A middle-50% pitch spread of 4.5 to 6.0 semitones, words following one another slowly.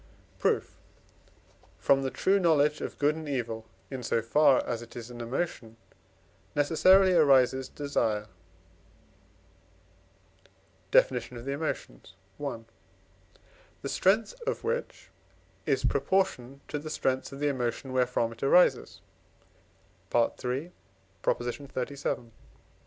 No: average, 4.0 semitones; slow, 110 wpm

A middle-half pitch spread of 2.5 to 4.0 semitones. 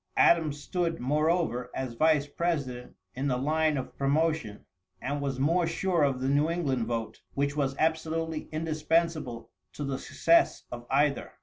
Yes: average, 3.4 semitones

